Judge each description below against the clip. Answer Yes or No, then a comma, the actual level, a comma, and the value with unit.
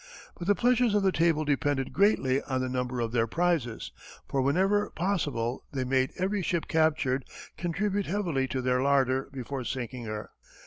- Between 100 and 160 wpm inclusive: No, average, 170 wpm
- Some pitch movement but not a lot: No, wide, 5.9 semitones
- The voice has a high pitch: No, medium, 140 Hz